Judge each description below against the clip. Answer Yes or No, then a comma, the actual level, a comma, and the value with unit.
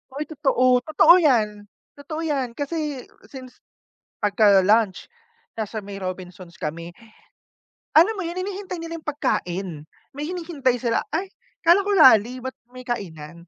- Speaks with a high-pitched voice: Yes, very high, 255 Hz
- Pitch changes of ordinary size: No, wide, 7.4 semitones